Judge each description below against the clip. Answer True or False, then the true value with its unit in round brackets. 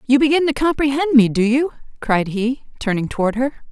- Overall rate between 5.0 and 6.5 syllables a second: True (5.6 syllables/s)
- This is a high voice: True (255 Hz)